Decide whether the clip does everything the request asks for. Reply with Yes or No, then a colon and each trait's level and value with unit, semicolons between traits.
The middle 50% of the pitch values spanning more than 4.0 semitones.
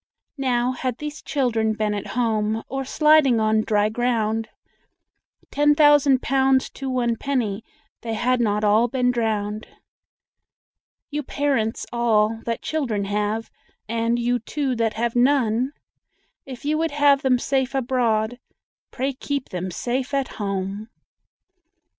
No: average, 3.7 semitones